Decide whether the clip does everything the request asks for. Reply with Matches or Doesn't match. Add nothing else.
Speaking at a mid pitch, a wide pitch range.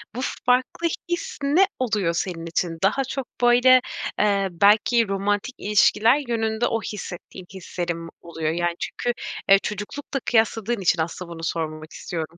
Doesn't match